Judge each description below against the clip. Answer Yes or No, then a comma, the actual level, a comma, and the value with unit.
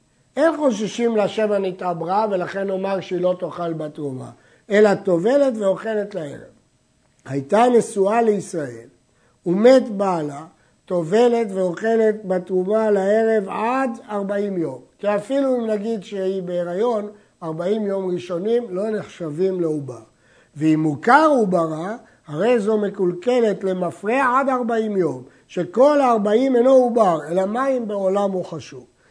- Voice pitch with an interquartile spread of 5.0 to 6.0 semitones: No, average, 4.3 semitones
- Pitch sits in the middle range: No, high, 195 Hz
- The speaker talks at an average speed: Yes, average, 115 wpm